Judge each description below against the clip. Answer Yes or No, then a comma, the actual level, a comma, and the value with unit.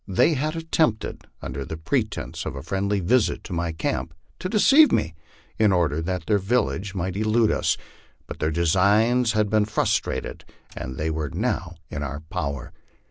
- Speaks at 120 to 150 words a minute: No, average, 165 wpm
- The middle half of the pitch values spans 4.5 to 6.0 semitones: Yes, wide, 5.4 semitones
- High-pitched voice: No, very low, 95 Hz